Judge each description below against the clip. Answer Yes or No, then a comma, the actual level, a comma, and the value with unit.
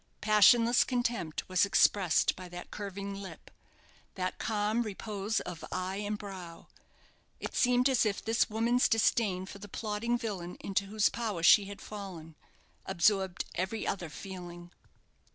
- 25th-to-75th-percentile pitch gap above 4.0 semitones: No, average, 3.1 semitones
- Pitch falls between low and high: No, high, 200 Hz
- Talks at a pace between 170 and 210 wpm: No, average, 140 wpm